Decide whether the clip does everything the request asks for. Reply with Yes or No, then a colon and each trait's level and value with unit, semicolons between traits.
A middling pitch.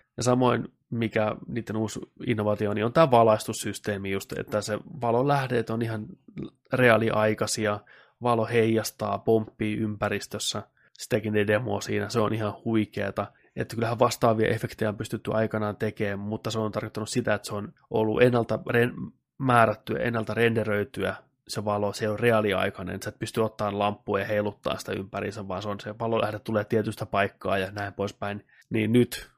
No: low, 110 Hz